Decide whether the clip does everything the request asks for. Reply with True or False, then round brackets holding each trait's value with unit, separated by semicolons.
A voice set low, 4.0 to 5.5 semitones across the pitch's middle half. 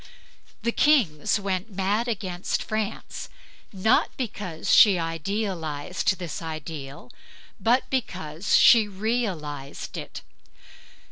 False (190 Hz; 5.2 semitones)